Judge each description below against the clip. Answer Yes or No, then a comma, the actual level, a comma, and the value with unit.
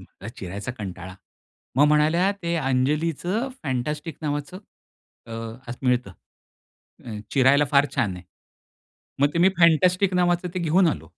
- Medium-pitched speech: Yes, medium, 145 Hz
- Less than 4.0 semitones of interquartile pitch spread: No, wide, 5.4 semitones